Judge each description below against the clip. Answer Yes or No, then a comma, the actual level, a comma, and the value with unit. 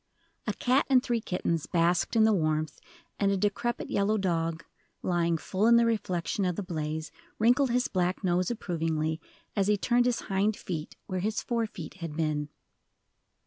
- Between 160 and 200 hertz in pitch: Yes, medium, 185 Hz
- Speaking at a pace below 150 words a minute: No, average, 175 wpm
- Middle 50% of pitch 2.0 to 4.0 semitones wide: No, average, 4.9 semitones